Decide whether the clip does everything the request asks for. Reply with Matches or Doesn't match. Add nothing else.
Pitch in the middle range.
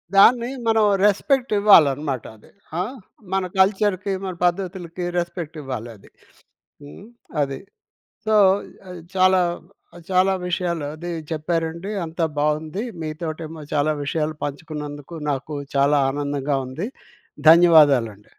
Matches